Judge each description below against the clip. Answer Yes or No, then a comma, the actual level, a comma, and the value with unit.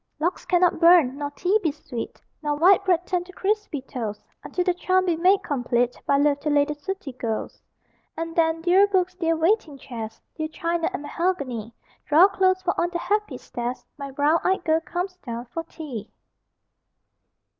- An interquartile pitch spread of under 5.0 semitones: Yes, average, 4.4 semitones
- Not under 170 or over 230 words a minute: Yes, average, 180 wpm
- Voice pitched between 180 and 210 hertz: No, very high, 325 Hz